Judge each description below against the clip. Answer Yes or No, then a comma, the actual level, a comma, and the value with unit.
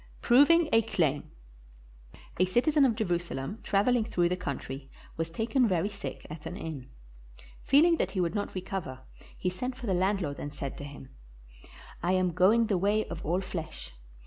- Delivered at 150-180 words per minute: Yes, average, 175 wpm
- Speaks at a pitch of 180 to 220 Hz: Yes, medium, 185 Hz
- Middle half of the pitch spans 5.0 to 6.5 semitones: Yes, wide, 5.6 semitones